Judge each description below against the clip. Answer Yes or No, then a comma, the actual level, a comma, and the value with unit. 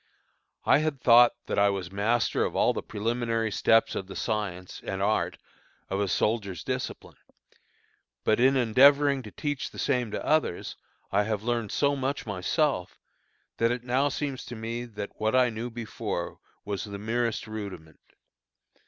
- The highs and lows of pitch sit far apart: No, average, 3.6 semitones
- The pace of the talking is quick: No, average, 160 wpm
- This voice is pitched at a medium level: No, low, 115 Hz